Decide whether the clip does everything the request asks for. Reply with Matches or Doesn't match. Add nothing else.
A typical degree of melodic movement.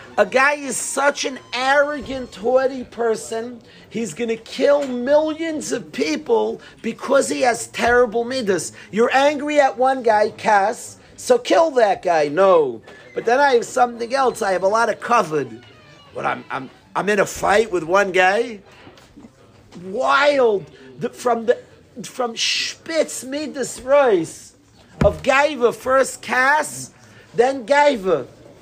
Matches